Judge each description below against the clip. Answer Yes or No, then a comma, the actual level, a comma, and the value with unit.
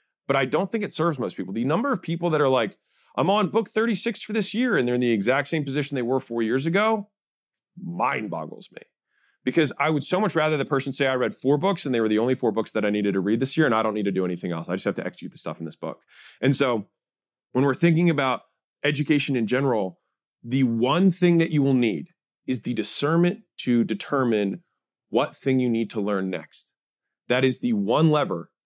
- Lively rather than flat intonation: Yes, wide, 6.7 semitones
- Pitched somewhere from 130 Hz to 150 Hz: Yes, low, 135 Hz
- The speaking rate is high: Yes, fast, 240 wpm